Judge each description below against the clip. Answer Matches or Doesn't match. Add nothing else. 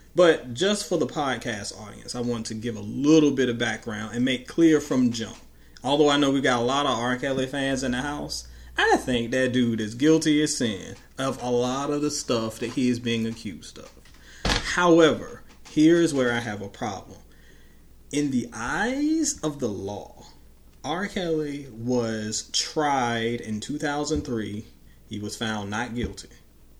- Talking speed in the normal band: Matches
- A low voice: Matches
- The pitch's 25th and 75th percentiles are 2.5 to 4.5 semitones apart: Doesn't match